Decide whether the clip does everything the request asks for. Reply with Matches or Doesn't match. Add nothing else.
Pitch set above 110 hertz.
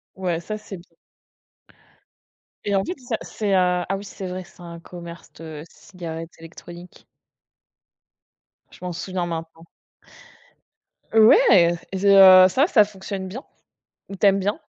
Matches